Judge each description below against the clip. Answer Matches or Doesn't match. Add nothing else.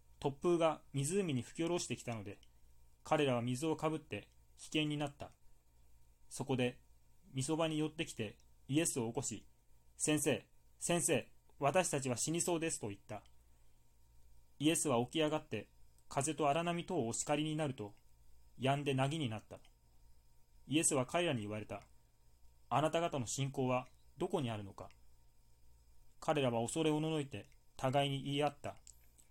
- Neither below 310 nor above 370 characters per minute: Doesn't match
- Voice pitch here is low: Matches